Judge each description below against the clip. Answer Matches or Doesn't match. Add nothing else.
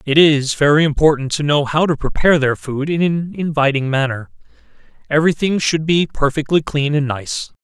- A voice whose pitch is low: Doesn't match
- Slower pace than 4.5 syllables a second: Doesn't match